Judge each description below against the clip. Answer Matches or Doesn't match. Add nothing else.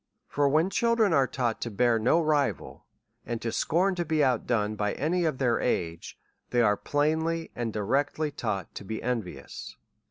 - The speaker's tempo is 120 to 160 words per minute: Doesn't match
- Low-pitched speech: Matches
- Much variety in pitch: Matches